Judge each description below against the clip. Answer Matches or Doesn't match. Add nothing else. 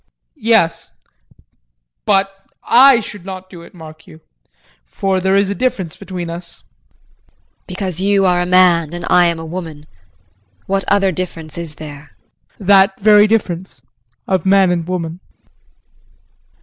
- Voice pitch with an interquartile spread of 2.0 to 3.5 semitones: Matches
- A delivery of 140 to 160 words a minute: Matches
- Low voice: Doesn't match